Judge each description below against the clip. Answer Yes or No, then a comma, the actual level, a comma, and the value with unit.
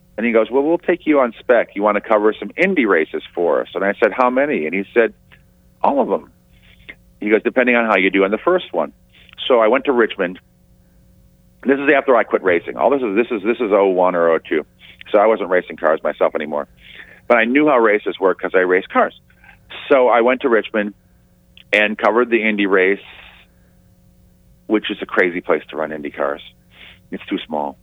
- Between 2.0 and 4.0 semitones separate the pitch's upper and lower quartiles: No, average, 4.4 semitones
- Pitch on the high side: No, low, 105 Hz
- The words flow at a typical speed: No, fast, 220 wpm